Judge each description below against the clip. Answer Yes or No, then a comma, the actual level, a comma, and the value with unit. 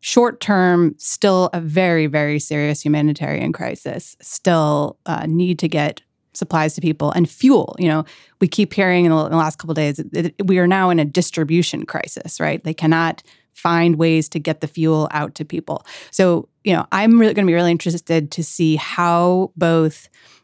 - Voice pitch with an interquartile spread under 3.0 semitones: Yes, narrow, 2.4 semitones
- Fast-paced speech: No, average, 190 wpm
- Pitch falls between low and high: Yes, medium, 165 Hz